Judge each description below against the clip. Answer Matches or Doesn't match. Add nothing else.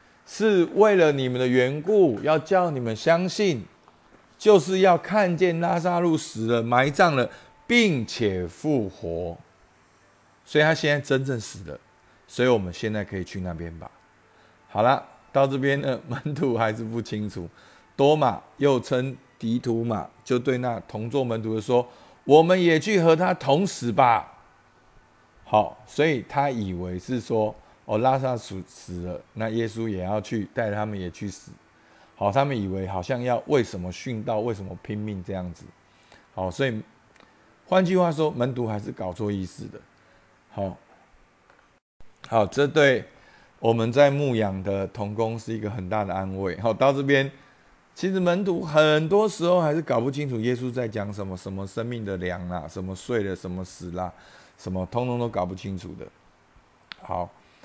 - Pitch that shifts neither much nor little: Doesn't match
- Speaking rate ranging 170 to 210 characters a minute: Doesn't match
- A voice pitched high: Doesn't match